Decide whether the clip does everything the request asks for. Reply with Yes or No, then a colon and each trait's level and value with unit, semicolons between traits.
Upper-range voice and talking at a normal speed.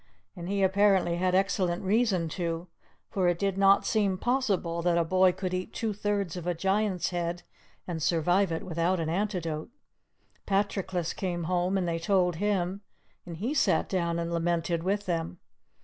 No: medium, 180 Hz; average, 170 wpm